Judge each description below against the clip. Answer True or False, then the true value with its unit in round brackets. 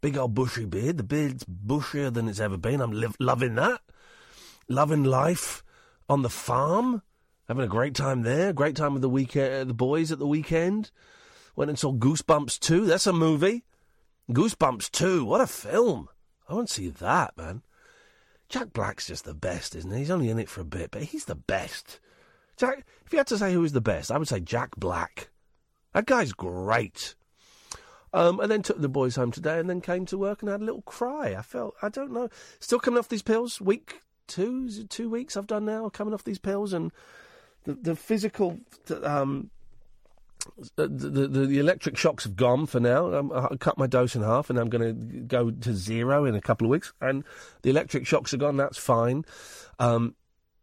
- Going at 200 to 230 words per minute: True (205 wpm)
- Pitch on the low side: False (145 Hz)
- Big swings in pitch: True (8.8 semitones)